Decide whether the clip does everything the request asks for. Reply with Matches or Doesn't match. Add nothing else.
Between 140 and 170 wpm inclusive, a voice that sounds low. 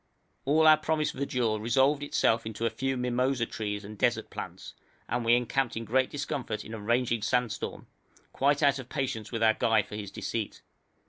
Doesn't match